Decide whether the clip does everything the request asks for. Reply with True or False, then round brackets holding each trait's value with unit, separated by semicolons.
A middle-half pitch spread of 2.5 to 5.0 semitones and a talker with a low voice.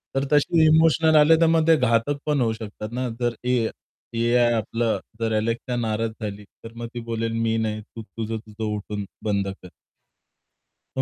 True (3.5 semitones; 115 Hz)